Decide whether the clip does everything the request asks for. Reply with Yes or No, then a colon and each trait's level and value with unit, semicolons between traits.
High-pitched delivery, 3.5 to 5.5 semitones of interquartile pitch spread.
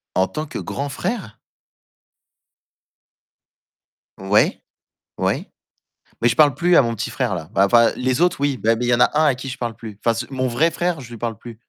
No: low, 125 Hz; average, 3.8 semitones